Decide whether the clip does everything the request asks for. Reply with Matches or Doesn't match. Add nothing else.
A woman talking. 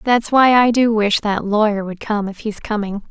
Matches